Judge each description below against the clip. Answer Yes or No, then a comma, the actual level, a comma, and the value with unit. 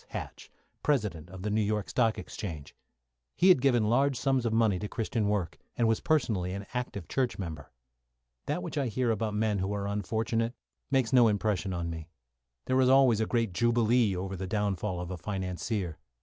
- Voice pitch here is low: Yes, low, 105 Hz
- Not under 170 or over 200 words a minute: Yes, average, 190 wpm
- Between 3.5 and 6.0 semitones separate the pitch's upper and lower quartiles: Yes, average, 4.0 semitones